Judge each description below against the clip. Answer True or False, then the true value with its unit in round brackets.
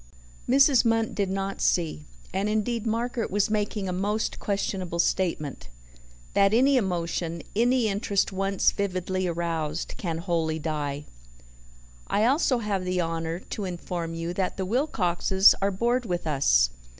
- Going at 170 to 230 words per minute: False (140 wpm)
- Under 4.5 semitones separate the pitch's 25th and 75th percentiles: True (4.1 semitones)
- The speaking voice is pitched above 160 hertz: True (190 Hz)